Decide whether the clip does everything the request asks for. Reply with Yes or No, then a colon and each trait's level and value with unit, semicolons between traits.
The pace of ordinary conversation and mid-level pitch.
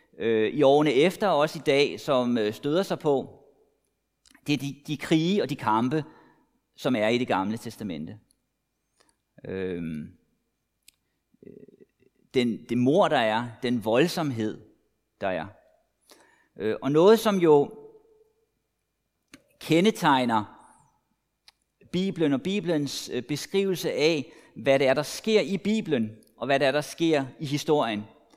No: slow, 125 wpm; medium, 145 Hz